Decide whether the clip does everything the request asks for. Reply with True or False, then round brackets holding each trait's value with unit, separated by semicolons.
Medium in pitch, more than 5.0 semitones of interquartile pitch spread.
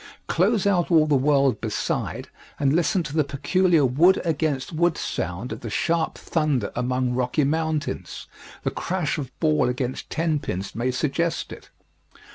False (150 Hz; 4.4 semitones)